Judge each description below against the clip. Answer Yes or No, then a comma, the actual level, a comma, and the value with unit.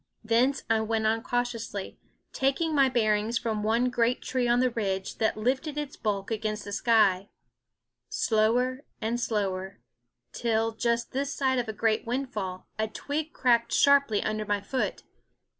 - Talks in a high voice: Yes, high, 230 Hz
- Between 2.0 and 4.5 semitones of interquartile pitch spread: Yes, average, 2.8 semitones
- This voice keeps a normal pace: Yes, average, 150 wpm